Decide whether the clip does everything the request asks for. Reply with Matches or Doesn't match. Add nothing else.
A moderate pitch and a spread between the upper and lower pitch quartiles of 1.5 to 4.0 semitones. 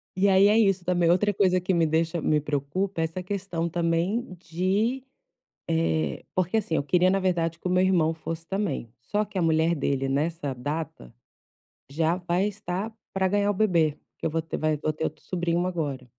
Matches